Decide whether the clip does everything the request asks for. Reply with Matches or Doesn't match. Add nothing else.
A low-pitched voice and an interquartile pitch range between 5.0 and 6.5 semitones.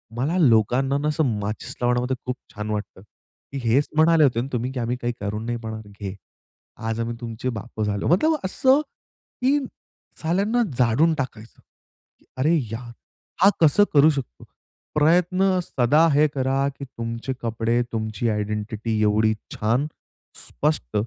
Matches